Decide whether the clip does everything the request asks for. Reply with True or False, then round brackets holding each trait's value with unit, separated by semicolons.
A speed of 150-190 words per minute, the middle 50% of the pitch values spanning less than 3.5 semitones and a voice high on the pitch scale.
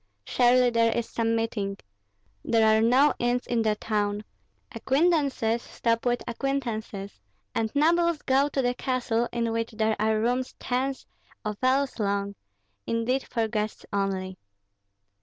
False (140 wpm; 2.9 semitones; 230 Hz)